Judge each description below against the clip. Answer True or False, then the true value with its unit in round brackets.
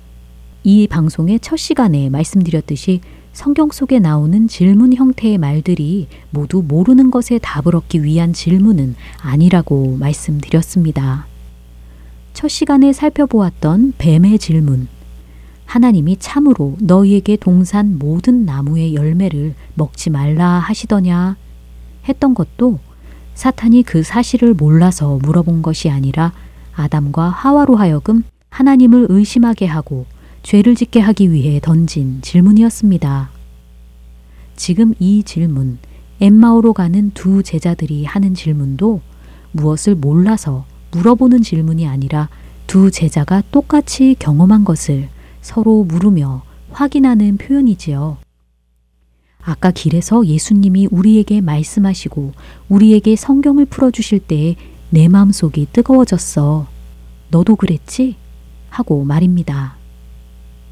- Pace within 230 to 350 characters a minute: True (265 characters per minute)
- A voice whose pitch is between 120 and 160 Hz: False (170 Hz)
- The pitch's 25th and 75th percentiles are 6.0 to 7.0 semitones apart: True (6.7 semitones)